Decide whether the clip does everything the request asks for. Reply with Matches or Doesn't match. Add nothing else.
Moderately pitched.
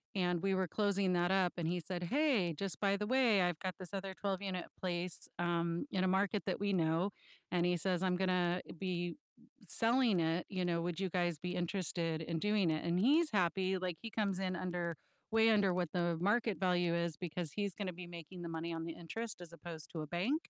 Matches